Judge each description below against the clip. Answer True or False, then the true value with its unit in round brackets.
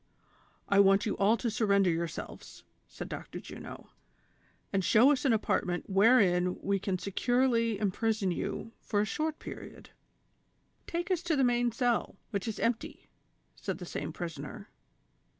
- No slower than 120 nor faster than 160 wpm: True (155 wpm)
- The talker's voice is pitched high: True (220 Hz)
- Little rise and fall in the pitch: False (3.7 semitones)